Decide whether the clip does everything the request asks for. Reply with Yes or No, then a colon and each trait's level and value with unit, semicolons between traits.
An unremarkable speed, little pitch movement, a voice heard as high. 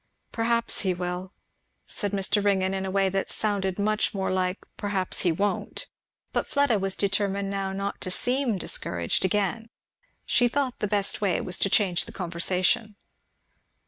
Yes: average, 160 wpm; narrow, 1.9 semitones; high, 195 Hz